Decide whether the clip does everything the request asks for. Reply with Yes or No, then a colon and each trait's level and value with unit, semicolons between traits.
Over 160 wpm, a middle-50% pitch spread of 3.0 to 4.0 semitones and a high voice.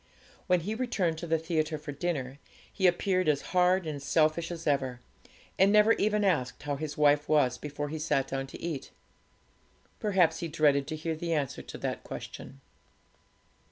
No: average, 175 wpm; average, 3.5 semitones; medium, 155 Hz